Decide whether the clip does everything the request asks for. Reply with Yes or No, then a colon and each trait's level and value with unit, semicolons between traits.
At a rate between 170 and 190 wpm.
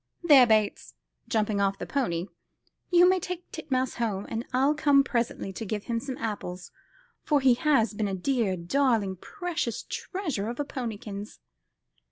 No: average, 160 wpm